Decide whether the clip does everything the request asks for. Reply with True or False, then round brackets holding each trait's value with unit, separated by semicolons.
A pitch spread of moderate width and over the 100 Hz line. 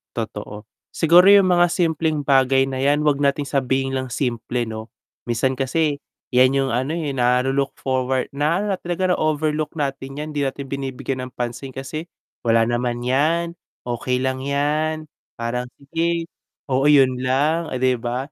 True (3.2 semitones; 135 Hz)